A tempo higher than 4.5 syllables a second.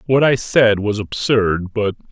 No: 3.8 syllables/s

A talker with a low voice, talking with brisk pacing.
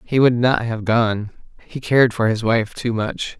Yes: low, 115 Hz; fast, 210 wpm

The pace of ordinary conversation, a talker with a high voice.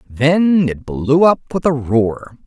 No: average, 170 wpm; medium, 140 Hz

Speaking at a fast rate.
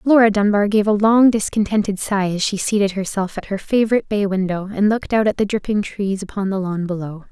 Yes: fast, 220 wpm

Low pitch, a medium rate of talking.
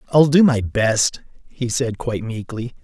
Yes: low, 120 Hz; average, 170 wpm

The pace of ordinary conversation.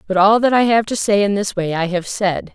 No: fast, 305 wpm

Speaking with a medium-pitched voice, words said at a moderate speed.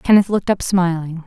Yes: medium, 180 Hz; average, 190 wpm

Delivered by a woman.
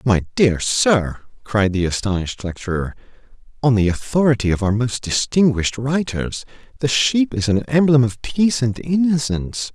No: male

